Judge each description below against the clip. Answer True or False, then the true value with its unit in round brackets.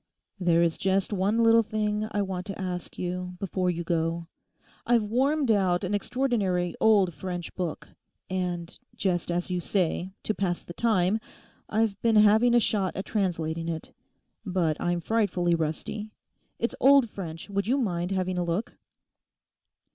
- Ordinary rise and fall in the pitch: True (3.4 semitones)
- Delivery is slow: False (150 wpm)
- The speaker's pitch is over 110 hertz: True (190 Hz)